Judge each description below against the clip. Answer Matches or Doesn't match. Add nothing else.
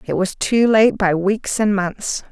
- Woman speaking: Matches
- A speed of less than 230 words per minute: Matches